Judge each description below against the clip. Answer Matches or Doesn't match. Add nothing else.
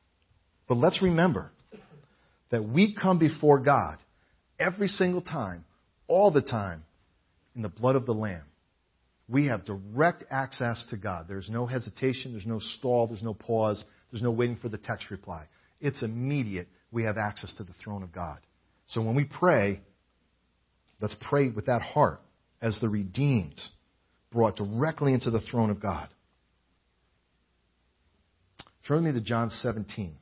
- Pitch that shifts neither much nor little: Doesn't match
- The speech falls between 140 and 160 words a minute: Matches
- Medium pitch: Doesn't match